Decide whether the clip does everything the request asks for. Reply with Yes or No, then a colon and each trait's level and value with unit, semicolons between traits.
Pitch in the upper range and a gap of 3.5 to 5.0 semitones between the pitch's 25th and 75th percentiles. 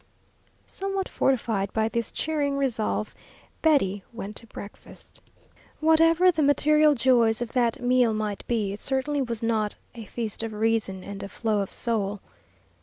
Yes: high, 230 Hz; average, 4.7 semitones